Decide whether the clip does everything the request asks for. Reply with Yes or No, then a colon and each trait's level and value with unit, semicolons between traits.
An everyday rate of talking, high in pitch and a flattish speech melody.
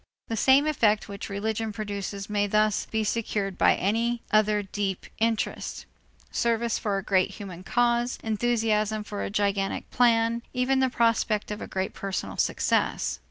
Yes: average, 155 wpm; high, 215 Hz; narrow, 2.3 semitones